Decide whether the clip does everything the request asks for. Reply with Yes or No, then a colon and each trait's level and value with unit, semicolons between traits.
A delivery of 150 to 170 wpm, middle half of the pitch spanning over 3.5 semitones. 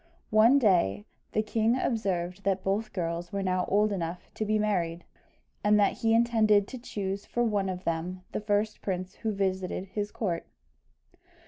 No: average, 165 wpm; average, 2.8 semitones